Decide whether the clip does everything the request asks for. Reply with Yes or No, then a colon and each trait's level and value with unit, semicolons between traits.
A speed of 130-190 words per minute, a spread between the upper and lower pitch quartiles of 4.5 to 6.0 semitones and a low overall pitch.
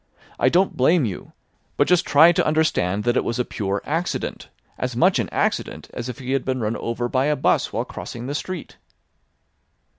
No: average, 200 wpm; average, 5.1 semitones; low, 130 Hz